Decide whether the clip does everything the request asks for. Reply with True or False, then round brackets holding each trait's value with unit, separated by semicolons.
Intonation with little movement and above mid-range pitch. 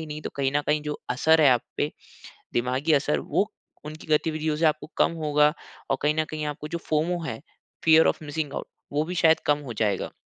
False (1.4 semitones; 150 Hz)